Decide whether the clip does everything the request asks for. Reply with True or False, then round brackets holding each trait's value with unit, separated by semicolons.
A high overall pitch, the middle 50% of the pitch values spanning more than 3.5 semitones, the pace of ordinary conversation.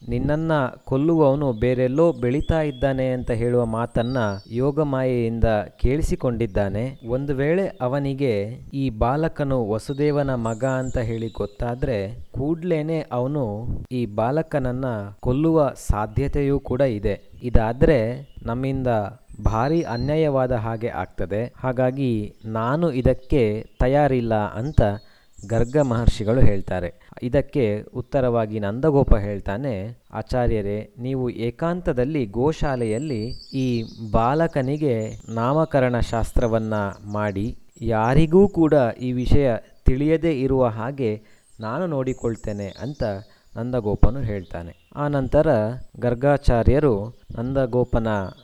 False (125 Hz; 4.1 semitones; 90 wpm)